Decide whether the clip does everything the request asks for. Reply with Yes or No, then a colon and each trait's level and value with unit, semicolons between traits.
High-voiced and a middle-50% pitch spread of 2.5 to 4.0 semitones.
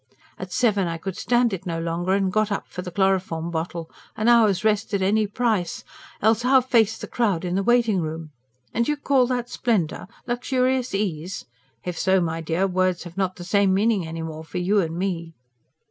No: high, 195 Hz; average, 4.4 semitones